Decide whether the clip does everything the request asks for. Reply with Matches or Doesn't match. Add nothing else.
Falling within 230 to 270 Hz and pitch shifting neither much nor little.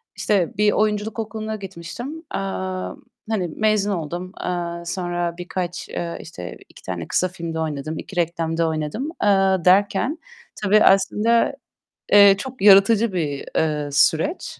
Doesn't match